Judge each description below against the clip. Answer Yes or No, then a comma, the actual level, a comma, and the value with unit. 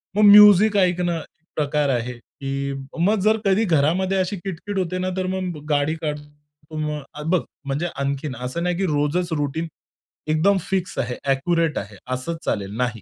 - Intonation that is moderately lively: Yes, average, 4.4 semitones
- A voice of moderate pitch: Yes, medium, 160 Hz